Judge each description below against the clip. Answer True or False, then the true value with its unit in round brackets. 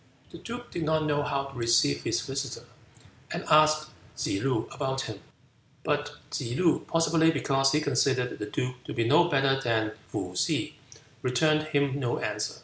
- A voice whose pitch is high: False (140 Hz)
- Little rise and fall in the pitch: False (3.8 semitones)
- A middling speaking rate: True (170 wpm)